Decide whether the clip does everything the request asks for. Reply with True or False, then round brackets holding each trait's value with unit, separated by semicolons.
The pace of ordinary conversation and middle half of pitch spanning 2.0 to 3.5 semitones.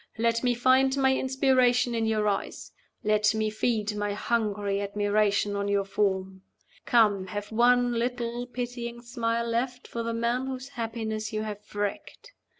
True (150 wpm; 2.8 semitones)